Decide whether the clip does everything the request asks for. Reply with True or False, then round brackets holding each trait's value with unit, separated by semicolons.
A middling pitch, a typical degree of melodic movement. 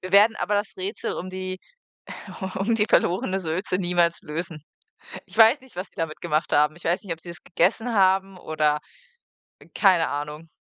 True (180 Hz; 3.0 semitones)